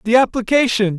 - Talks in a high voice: Yes, high, 230 Hz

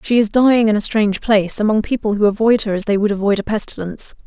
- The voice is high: Yes, high, 210 Hz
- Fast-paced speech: Yes, fast, 255 wpm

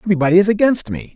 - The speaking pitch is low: No, medium, 185 Hz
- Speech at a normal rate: No, fast, 210 wpm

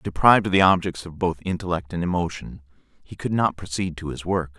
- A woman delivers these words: No, male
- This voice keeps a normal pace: No, fast, 210 wpm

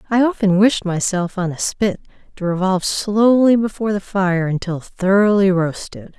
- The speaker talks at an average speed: Yes, average, 155 wpm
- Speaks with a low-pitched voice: No, high, 195 Hz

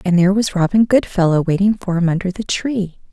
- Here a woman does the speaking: Yes, female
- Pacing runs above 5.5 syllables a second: Yes, 5.8 syllables/s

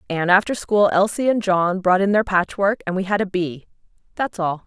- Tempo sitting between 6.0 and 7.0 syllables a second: No, 5.1 syllables/s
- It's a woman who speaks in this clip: Yes, female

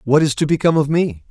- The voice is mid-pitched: Yes, medium, 145 Hz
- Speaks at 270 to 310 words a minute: Yes, fast, 275 wpm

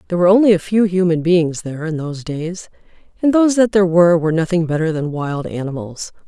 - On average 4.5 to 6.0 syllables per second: No, 6.6 syllables/s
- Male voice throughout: No, female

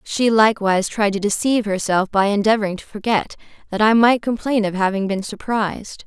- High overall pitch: Yes, high, 210 Hz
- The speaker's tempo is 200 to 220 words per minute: No, average, 180 wpm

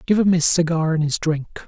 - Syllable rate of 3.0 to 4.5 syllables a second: No, 5.2 syllables/s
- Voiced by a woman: No, male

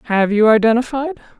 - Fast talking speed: No, slow, 130 wpm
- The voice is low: No, high, 235 Hz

